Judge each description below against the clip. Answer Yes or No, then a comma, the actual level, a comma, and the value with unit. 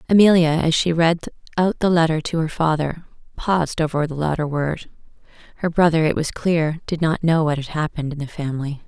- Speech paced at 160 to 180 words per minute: No, average, 195 wpm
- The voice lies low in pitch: No, medium, 160 Hz